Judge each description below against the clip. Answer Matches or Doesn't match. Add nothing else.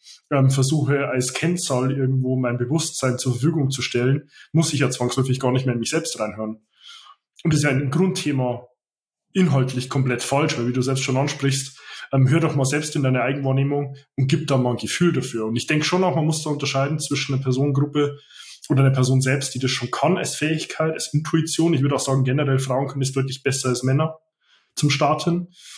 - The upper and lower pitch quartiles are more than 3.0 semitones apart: Doesn't match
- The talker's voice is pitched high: Doesn't match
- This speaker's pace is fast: Matches